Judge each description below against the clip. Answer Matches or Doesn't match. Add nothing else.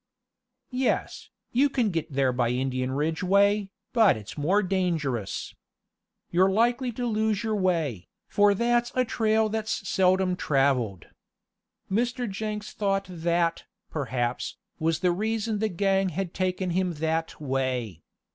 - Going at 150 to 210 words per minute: Doesn't match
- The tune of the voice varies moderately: Doesn't match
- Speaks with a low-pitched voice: Doesn't match